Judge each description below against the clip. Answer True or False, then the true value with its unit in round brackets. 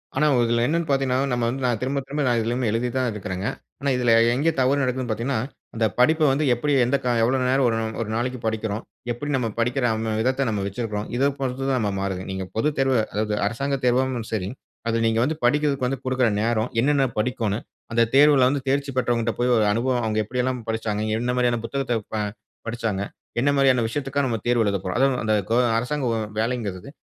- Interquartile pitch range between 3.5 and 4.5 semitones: False (3.0 semitones)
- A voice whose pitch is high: False (125 Hz)